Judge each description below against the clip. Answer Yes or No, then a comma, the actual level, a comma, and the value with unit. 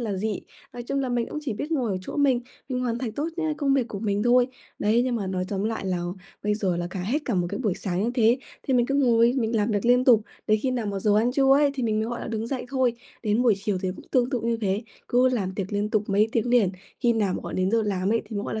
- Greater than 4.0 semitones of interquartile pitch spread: No, average, 3.4 semitones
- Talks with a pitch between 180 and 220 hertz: No, high, 230 Hz